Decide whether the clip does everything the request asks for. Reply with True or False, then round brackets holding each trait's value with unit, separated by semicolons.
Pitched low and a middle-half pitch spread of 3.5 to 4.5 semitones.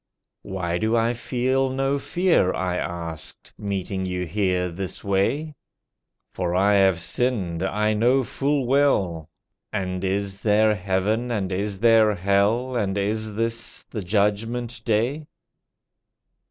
True (105 Hz; 4.0 semitones)